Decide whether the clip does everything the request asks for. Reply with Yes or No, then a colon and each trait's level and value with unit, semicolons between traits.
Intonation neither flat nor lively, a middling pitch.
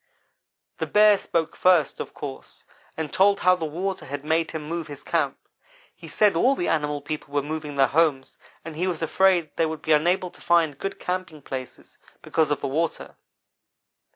Yes: average, 3.5 semitones; medium, 160 Hz